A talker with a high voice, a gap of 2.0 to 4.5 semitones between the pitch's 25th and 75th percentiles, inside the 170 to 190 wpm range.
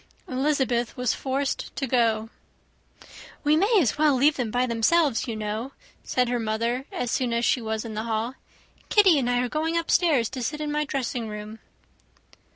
Yes: very high, 250 Hz; average, 4.2 semitones; average, 180 wpm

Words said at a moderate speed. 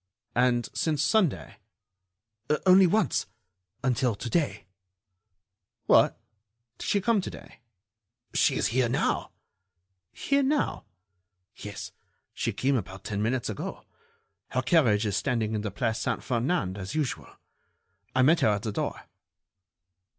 No: slow, 130 wpm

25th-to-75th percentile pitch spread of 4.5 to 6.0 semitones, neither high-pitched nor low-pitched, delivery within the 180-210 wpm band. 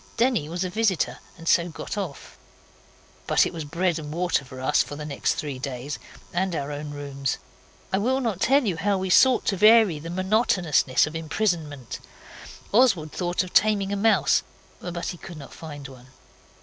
Yes: average, 5.2 semitones; medium, 175 Hz; average, 185 wpm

